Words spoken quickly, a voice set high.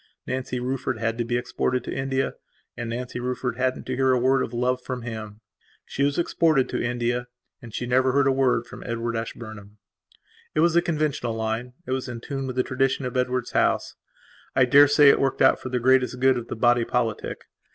No: fast, 210 wpm; low, 125 Hz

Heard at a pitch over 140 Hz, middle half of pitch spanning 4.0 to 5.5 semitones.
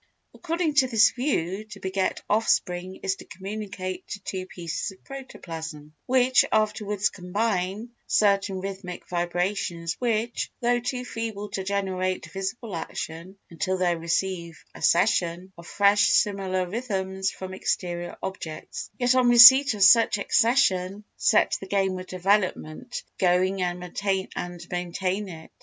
No: high, 190 Hz; average, 3.1 semitones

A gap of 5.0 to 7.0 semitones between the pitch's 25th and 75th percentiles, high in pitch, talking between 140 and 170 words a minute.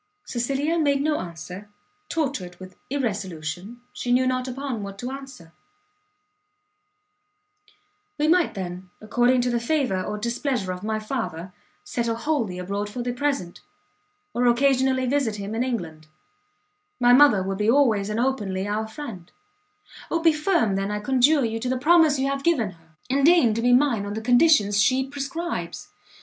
Yes: average, 5.3 semitones; high, 240 Hz; average, 160 wpm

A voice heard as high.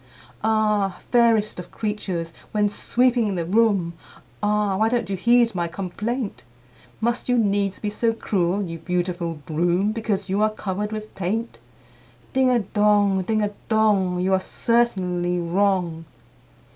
Yes: high, 205 Hz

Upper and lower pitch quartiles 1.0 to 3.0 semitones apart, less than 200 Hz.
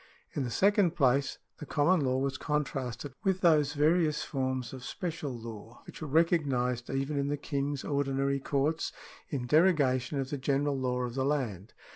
Yes: average, 2.7 semitones; medium, 140 Hz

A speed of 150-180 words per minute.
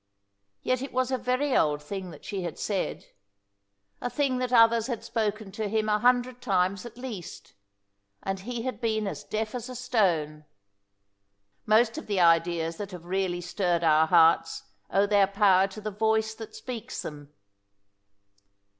Yes: average, 165 wpm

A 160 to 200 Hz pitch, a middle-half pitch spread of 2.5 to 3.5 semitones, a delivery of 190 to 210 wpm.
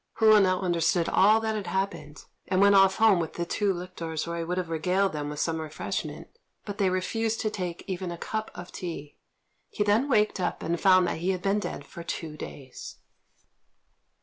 Yes: medium, 185 Hz; average, 3.2 semitones; fast, 205 wpm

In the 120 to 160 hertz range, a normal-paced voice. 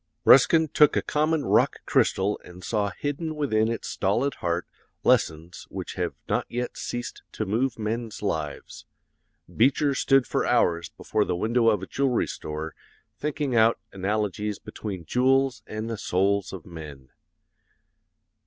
No: low, 110 Hz; average, 145 wpm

